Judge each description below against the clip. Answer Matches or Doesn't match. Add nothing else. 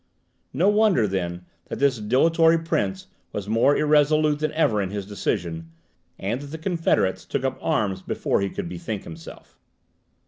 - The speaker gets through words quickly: Doesn't match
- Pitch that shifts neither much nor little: Doesn't match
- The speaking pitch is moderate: Doesn't match